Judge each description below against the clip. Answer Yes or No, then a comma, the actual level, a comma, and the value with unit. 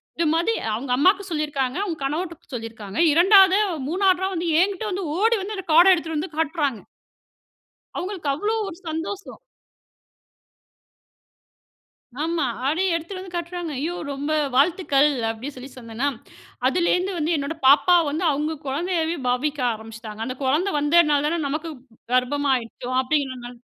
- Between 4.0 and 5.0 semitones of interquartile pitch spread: Yes, average, 4.7 semitones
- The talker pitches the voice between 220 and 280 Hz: No, very high, 315 Hz